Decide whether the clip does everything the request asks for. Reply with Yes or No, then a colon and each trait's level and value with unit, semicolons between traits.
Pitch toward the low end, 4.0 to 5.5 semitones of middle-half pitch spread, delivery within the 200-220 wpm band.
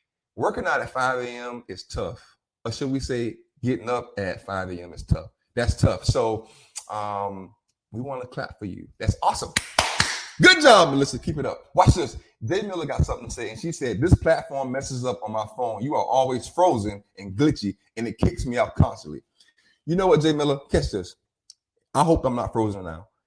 Yes: low, 120 Hz; average, 4.8 semitones; fast, 205 wpm